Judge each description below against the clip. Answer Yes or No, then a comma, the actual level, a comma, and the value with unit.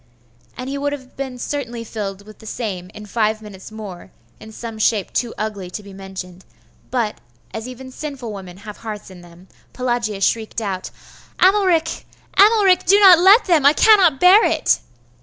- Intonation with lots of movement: Yes, wide, 6.0 semitones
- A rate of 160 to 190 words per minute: Yes, average, 175 wpm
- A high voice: Yes, high, 230 Hz